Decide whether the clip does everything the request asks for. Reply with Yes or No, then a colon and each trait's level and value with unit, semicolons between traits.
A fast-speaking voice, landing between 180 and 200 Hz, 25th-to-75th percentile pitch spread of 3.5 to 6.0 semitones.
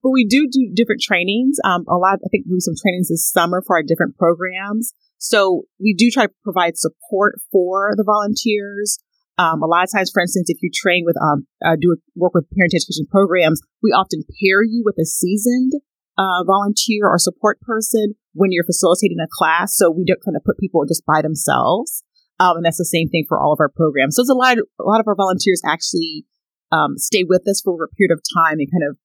Yes: fast, 235 wpm; high, 190 Hz; average, 3.8 semitones